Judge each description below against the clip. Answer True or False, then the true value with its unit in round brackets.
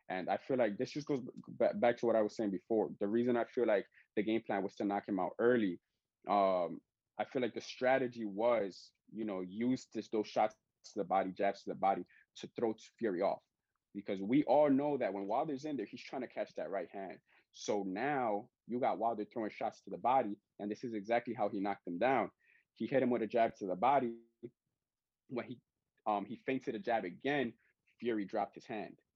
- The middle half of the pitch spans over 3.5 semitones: False (3.0 semitones)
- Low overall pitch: True (115 Hz)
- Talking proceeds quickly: True (220 wpm)